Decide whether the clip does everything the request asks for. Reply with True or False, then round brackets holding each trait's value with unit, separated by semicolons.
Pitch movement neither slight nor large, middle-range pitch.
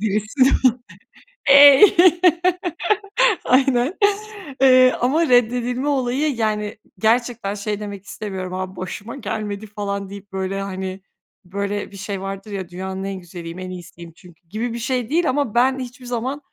False (4.5 semitones; 210 Hz)